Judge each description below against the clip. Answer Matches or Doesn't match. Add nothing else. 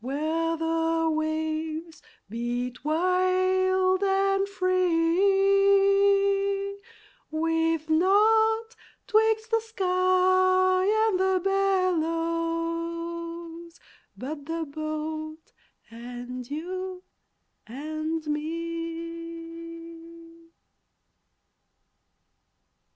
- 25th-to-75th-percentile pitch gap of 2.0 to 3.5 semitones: Matches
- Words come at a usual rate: Doesn't match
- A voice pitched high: Matches